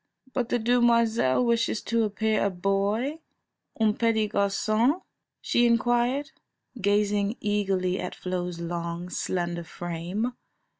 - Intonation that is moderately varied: Yes, average, 4.2 semitones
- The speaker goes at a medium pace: No, slow, 110 wpm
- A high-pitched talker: Yes, high, 210 Hz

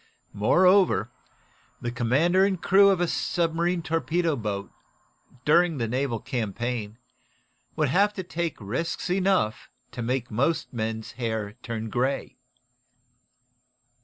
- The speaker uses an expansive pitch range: Yes, wide, 7.4 semitones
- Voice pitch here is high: No, low, 135 Hz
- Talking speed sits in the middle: No, slow, 115 wpm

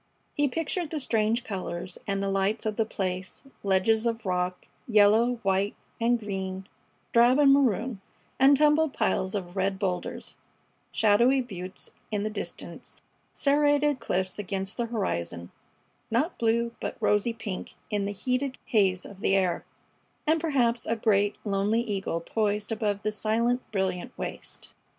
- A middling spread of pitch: Yes, average, 3.8 semitones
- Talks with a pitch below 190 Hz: No, high, 215 Hz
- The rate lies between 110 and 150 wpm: Yes, average, 145 wpm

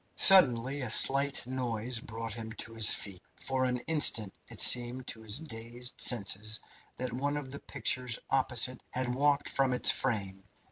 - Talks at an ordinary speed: Yes, average, 160 wpm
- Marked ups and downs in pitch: No, average, 2.9 semitones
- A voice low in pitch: Yes, low, 125 Hz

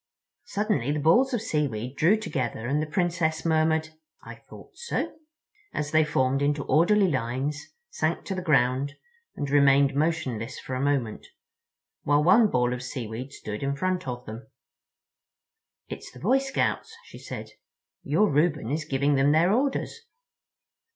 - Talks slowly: No, average, 150 wpm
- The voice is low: No, medium, 145 Hz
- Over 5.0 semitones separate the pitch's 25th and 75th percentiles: No, average, 4.7 semitones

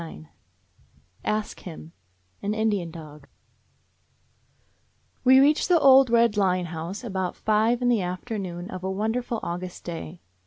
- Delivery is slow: No, average, 145 wpm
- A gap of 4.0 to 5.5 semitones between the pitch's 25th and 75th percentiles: Yes, average, 5.1 semitones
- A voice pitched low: No, high, 195 Hz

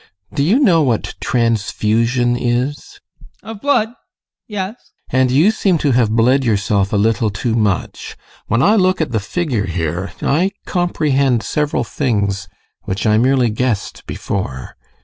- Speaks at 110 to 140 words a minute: No, average, 150 wpm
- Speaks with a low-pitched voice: Yes, low, 125 Hz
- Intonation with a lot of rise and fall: Yes, wide, 6.3 semitones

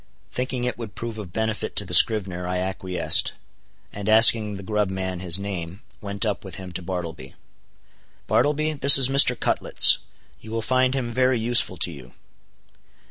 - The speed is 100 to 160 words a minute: No, average, 170 wpm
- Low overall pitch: Yes, low, 105 Hz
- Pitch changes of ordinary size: Yes, average, 4.6 semitones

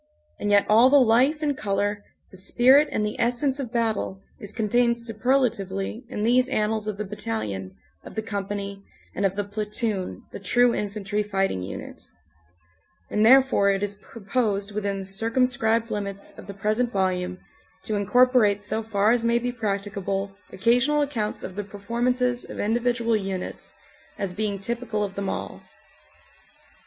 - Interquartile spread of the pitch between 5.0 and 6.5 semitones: No, average, 3.2 semitones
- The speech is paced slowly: No, average, 160 wpm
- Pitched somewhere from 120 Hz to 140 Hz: No, high, 210 Hz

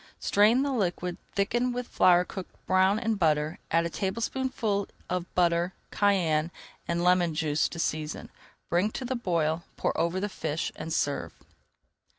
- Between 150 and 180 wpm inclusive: Yes, average, 155 wpm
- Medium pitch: Yes, medium, 180 Hz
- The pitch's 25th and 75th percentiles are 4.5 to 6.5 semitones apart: No, average, 3.7 semitones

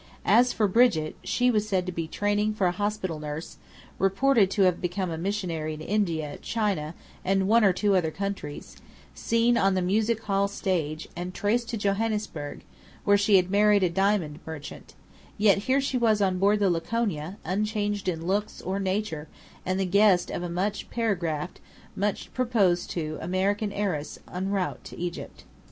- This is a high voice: Yes, high, 195 Hz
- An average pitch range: Yes, average, 3.1 semitones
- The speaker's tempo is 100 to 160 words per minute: No, average, 175 wpm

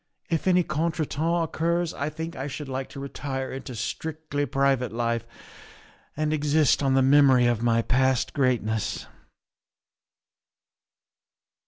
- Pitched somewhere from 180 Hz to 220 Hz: No, medium, 140 Hz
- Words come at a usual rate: No, slow, 125 wpm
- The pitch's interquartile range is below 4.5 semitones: Yes, average, 3.4 semitones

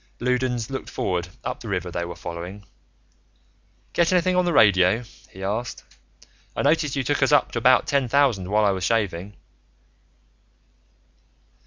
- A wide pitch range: Yes, wide, 6.6 semitones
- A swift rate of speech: No, average, 155 wpm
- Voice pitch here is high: No, low, 115 Hz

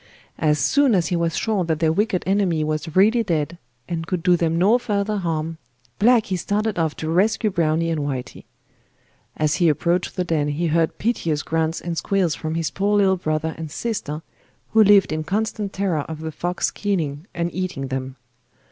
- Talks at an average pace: Yes, average, 185 wpm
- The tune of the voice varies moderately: Yes, average, 4.0 semitones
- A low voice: No, medium, 170 Hz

